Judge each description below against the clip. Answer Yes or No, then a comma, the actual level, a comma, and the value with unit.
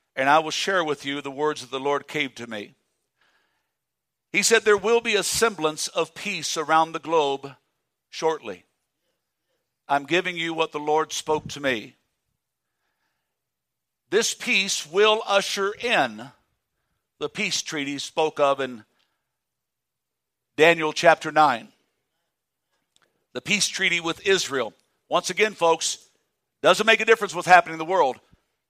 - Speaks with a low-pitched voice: No, medium, 160 Hz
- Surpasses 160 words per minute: No, average, 140 wpm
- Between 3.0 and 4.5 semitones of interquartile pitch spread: No, wide, 5.4 semitones